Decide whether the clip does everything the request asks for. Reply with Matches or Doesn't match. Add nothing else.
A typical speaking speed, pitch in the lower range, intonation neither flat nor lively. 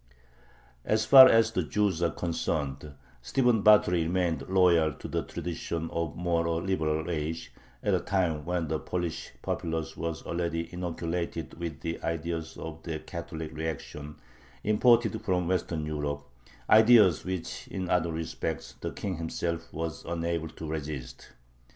Doesn't match